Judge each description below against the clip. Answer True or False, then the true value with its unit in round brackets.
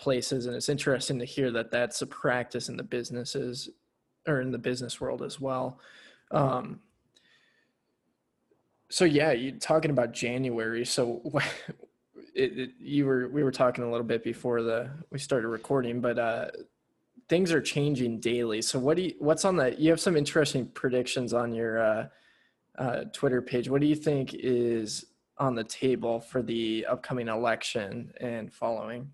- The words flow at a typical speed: True (165 wpm)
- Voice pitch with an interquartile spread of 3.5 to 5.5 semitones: False (3.1 semitones)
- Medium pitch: False (125 Hz)